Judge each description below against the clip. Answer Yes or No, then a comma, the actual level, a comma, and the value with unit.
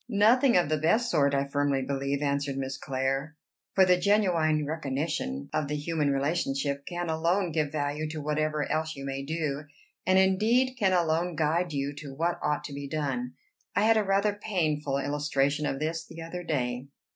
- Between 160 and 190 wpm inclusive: Yes, average, 180 wpm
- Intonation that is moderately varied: Yes, average, 3.8 semitones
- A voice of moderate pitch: Yes, medium, 155 Hz